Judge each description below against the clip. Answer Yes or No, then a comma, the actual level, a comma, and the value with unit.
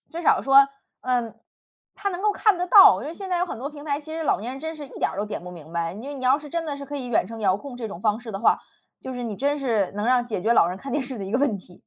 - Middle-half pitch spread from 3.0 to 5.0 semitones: No, wide, 5.6 semitones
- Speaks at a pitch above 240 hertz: Yes, very high, 255 Hz